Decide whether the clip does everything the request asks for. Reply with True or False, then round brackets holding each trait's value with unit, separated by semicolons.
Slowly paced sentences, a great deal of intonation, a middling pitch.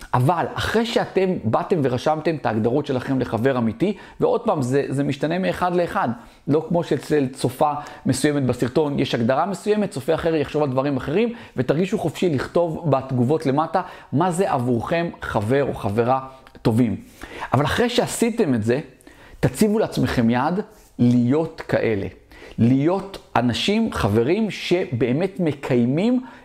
False (135 wpm; 5.9 semitones; 150 Hz)